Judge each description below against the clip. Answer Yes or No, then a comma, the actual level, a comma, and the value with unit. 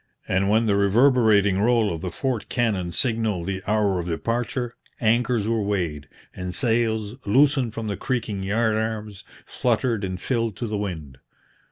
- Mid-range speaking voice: No, low, 110 Hz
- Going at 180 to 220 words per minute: No, average, 160 wpm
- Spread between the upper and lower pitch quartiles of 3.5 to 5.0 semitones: No, average, 3.1 semitones